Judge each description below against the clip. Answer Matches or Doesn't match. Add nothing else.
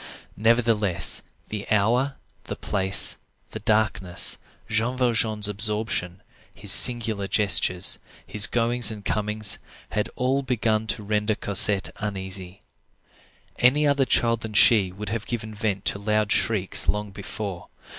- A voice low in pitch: Matches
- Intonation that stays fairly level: Matches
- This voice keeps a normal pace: Doesn't match